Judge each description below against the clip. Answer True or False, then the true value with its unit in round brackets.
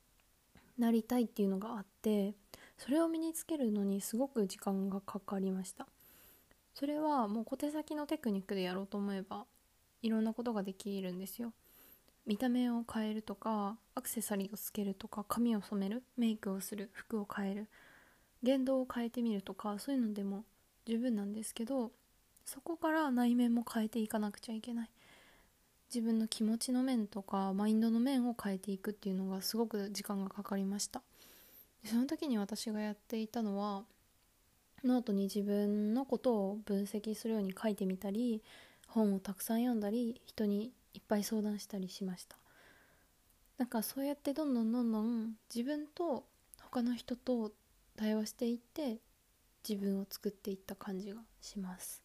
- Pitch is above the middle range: True (220 Hz)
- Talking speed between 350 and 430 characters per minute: True (355 characters per minute)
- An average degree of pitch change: True (3.1 semitones)